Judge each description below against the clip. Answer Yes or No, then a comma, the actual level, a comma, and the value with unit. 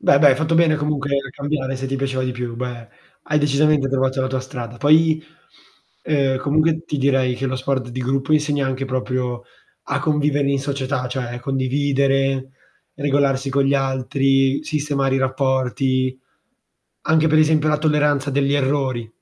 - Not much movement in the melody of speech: Yes, narrow, 1.8 semitones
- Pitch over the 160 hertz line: No, low, 135 Hz